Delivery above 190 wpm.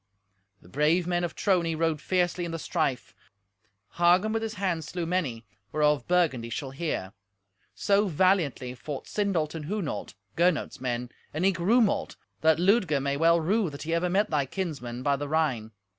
No: average, 170 wpm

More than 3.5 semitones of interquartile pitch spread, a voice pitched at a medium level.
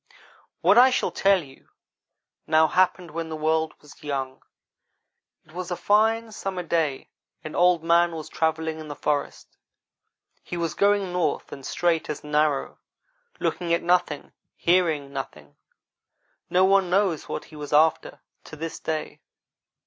No: average, 3.0 semitones; medium, 160 Hz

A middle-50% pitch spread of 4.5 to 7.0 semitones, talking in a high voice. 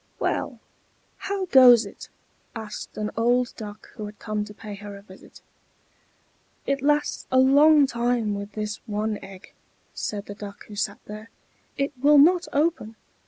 Yes: average, 4.8 semitones; high, 220 Hz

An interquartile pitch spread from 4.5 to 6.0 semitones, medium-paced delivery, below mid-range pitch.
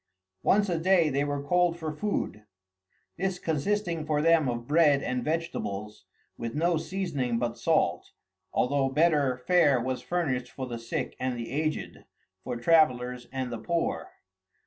No: average, 5.1 semitones; average, 155 wpm; medium, 145 Hz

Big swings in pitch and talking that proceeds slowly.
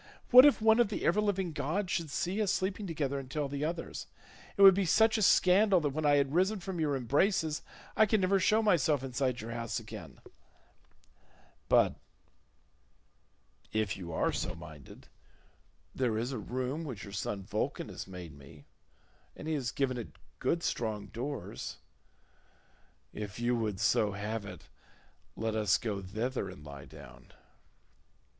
No: wide, 9.0 semitones; average, 165 wpm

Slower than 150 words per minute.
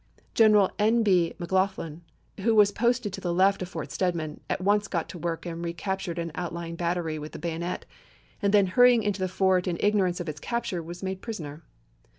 No: average, 200 wpm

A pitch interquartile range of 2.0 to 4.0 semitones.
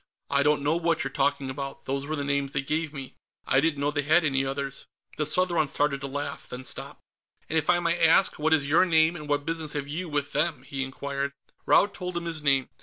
Yes: narrow, 2.6 semitones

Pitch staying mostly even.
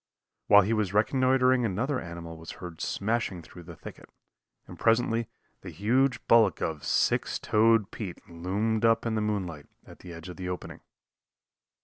No: average, 4.4 semitones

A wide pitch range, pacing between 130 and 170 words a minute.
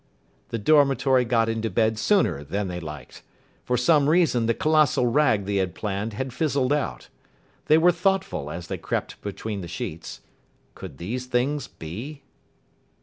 Yes: wide, 6.5 semitones; average, 155 wpm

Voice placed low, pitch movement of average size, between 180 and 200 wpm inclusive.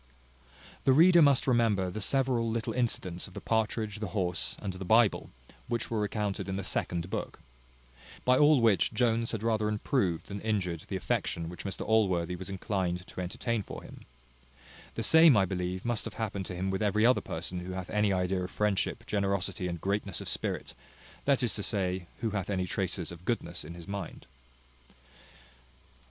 Yes: low, 100 Hz; average, 3.7 semitones; average, 185 wpm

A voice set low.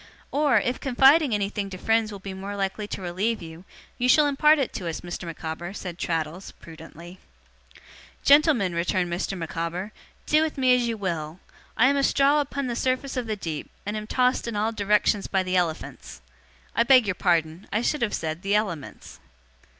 No: high, 205 Hz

